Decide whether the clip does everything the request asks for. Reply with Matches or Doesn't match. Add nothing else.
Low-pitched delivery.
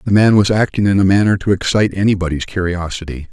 Matches